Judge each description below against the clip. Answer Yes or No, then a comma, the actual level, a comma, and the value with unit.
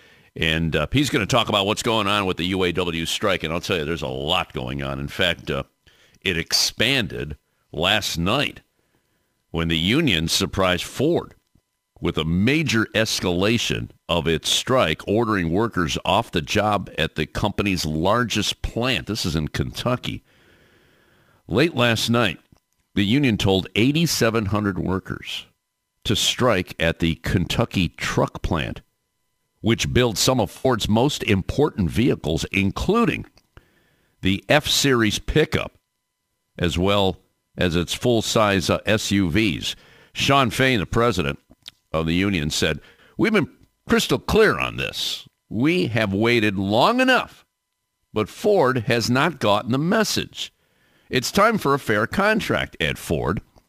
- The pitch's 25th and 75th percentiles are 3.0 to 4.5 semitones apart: No, wide, 5.6 semitones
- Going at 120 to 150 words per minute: Yes, average, 140 wpm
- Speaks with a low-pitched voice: Yes, low, 100 Hz